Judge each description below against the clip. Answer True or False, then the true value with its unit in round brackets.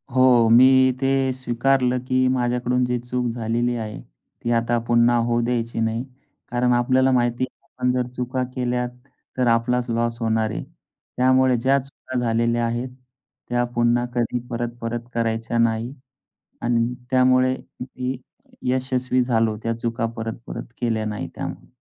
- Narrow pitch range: True (1.4 semitones)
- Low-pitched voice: True (120 Hz)